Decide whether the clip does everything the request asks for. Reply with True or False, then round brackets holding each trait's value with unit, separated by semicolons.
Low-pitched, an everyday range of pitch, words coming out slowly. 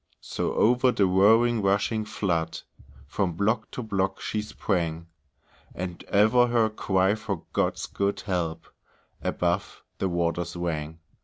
True (100 Hz; 4.0 semitones; 130 wpm)